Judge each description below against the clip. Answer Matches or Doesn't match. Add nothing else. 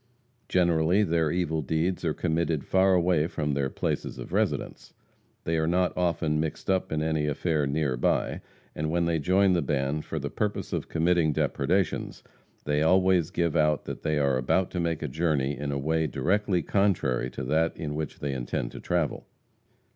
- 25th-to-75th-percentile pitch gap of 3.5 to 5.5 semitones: Doesn't match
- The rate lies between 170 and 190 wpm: Matches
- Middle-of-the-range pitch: Doesn't match